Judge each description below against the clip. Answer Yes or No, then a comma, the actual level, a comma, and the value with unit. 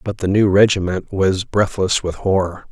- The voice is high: No, very low, 95 Hz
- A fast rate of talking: No, average, 175 wpm